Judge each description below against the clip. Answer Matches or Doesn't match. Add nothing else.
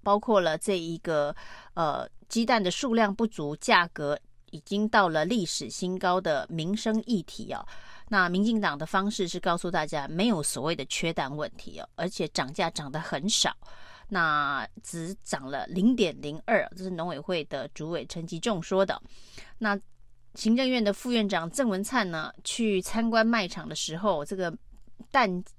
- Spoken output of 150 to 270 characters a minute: Matches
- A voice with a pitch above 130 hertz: Matches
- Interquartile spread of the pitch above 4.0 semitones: Matches